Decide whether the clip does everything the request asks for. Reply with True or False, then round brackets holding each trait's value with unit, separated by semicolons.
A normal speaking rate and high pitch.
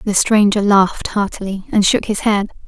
True (180 wpm; 200 Hz)